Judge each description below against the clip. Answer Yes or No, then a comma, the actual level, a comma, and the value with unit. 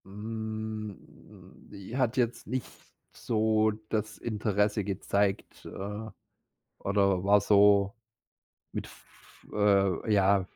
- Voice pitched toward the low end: Yes, low, 105 Hz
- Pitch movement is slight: Yes, narrow, 1.7 semitones